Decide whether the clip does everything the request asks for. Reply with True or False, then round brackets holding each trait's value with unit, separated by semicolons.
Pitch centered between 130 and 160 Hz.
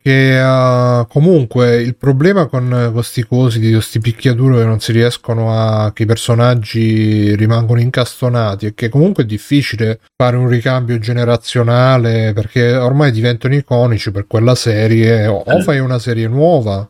False (120 Hz)